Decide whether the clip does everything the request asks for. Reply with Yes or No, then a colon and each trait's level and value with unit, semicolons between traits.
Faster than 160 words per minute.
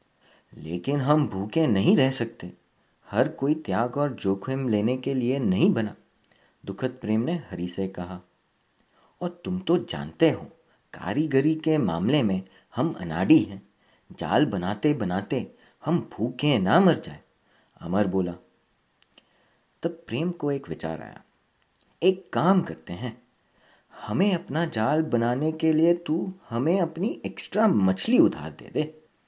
No: average, 140 wpm